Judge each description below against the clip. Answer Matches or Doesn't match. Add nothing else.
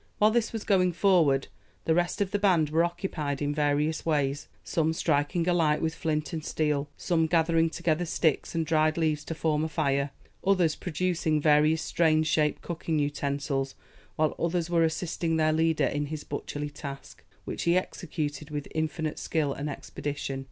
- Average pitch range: Doesn't match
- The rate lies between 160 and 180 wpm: Matches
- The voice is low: Doesn't match